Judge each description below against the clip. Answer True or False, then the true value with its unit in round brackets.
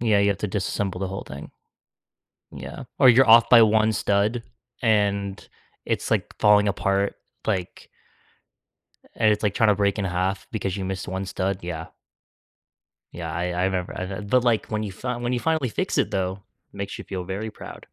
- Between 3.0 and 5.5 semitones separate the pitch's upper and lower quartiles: False (2.6 semitones)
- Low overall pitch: True (100 Hz)